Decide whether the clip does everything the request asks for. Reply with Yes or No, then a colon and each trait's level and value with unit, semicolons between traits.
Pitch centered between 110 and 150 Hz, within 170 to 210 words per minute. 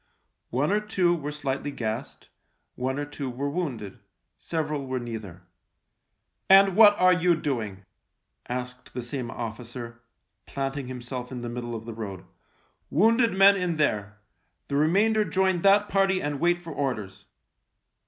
No: medium, 140 Hz; average, 155 wpm